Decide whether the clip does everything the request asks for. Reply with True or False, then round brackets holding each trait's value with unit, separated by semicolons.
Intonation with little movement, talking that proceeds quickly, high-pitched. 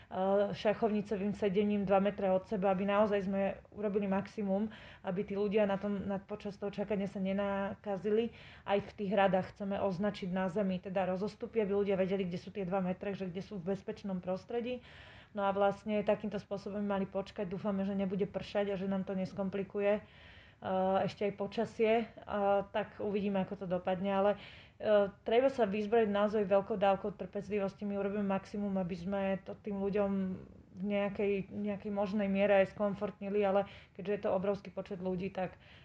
True (1.1 semitones; 170 wpm; 200 Hz)